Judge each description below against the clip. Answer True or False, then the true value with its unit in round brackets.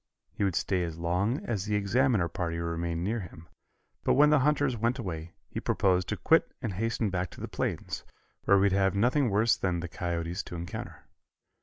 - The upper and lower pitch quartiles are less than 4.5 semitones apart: False (4.8 semitones)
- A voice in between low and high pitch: False (95 Hz)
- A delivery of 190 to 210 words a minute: True (200 wpm)